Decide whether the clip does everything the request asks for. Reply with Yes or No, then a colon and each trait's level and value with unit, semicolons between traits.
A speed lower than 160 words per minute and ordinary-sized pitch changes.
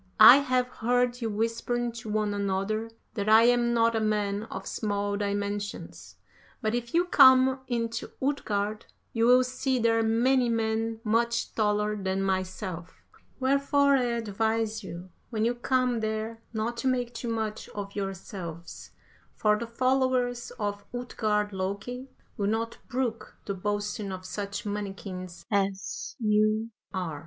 Yes: average, 145 wpm; average, 3.0 semitones